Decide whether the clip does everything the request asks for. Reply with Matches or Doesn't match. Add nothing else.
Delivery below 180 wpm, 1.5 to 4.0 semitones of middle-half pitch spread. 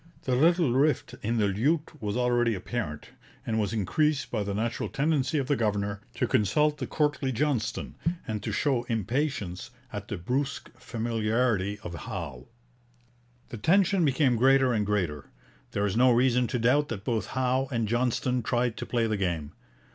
Doesn't match